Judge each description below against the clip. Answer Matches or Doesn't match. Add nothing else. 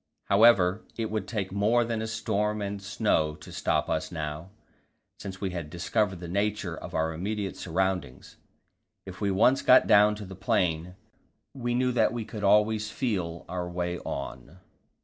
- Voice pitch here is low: Matches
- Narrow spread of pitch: Doesn't match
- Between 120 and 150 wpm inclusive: Doesn't match